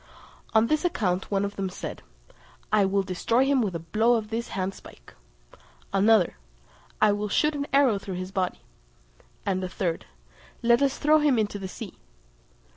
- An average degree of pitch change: Yes, average, 4.1 semitones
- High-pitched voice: Yes, high, 205 Hz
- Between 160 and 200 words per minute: Yes, average, 170 wpm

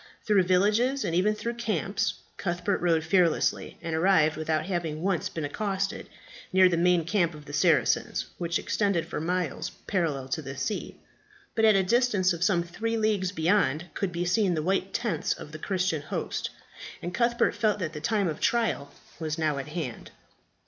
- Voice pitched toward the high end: No, medium, 180 Hz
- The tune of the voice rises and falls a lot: No, average, 4.2 semitones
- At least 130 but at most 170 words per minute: No, average, 180 wpm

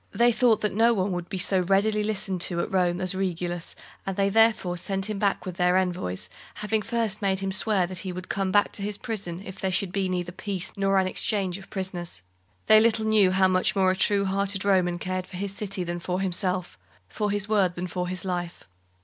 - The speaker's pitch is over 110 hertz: Yes, high, 190 Hz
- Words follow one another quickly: Yes, fast, 225 wpm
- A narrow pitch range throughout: Yes, narrow, 2.0 semitones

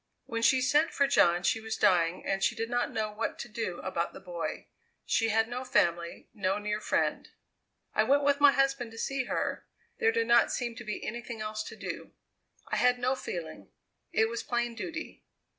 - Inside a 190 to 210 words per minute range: Yes, average, 200 wpm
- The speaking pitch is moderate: No, high, 235 Hz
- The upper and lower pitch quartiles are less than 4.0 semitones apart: Yes, average, 3.6 semitones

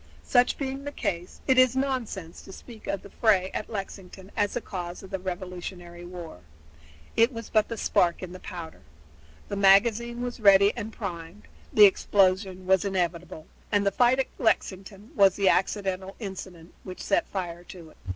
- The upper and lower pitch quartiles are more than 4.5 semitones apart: No, average, 3.3 semitones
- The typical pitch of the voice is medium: No, high, 195 Hz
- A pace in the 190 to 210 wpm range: No, average, 175 wpm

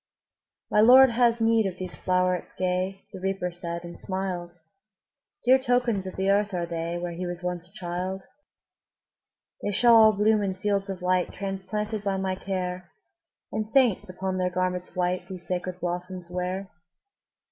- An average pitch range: No, narrow, 2.3 semitones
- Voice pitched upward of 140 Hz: Yes, medium, 185 Hz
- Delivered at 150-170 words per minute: Yes, average, 165 wpm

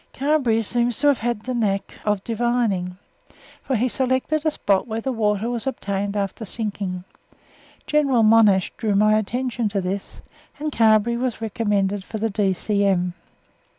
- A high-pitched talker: Yes, high, 220 Hz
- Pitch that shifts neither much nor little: Yes, average, 3.3 semitones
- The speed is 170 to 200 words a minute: No, average, 145 wpm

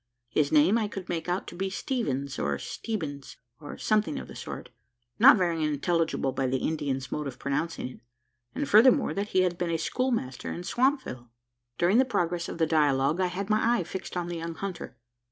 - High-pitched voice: No, medium, 170 Hz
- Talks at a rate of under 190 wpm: No, average, 200 wpm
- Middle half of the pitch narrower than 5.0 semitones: No, wide, 5.5 semitones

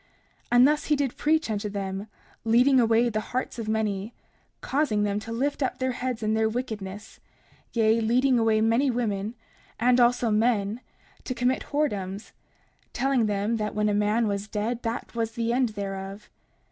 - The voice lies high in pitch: Yes, high, 225 Hz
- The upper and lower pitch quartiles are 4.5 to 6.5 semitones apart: No, average, 2.9 semitones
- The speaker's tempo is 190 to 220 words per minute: No, average, 170 wpm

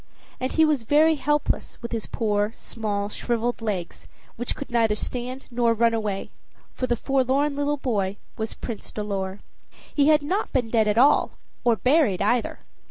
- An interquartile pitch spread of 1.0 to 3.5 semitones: No, average, 4.4 semitones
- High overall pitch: Yes, high, 235 Hz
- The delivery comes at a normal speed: Yes, average, 165 wpm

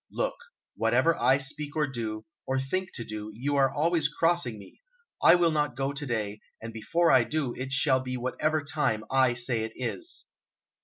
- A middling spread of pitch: Yes, average, 4.2 semitones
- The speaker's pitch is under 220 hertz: Yes, low, 135 Hz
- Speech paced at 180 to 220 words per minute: Yes, average, 190 wpm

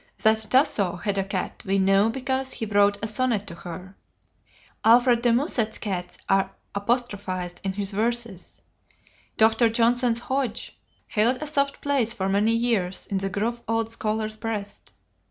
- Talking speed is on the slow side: No, average, 155 wpm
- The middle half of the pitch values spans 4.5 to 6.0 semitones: No, average, 3.3 semitones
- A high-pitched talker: Yes, high, 220 Hz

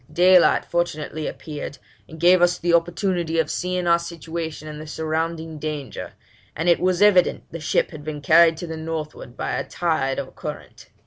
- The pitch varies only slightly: Yes, narrow, 1.9 semitones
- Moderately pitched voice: Yes, medium, 165 Hz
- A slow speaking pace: No, average, 180 wpm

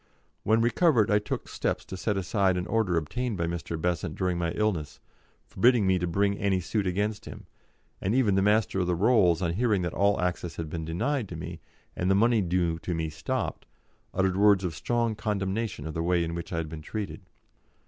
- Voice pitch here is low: Yes, very low, 95 Hz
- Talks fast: Yes, fast, 210 wpm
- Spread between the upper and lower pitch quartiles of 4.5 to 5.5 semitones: No, average, 3.8 semitones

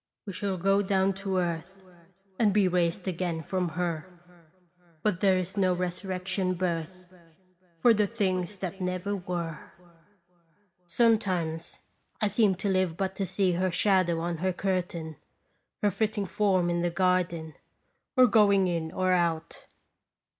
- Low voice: No, medium, 185 Hz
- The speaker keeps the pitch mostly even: Yes, narrow, 2.2 semitones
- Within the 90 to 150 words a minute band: Yes, average, 145 wpm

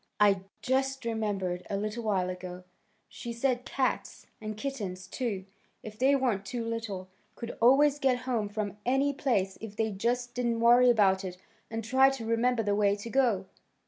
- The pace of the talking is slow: No, average, 175 wpm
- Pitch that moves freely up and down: No, average, 3.7 semitones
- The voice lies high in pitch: Yes, high, 225 Hz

